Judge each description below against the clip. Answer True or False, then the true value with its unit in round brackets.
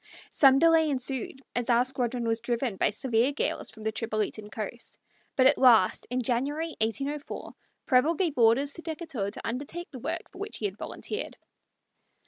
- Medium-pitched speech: False (255 Hz)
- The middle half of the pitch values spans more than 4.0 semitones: True (4.4 semitones)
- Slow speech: False (170 wpm)